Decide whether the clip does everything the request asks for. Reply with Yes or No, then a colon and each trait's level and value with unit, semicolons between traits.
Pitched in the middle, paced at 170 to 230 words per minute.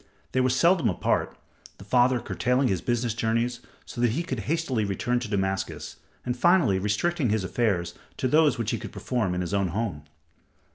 No: low, 120 Hz; average, 185 wpm